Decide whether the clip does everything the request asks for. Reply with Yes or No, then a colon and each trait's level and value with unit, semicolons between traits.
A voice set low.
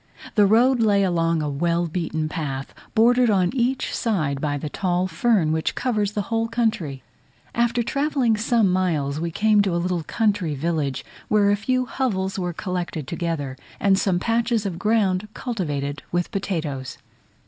No: medium, 185 Hz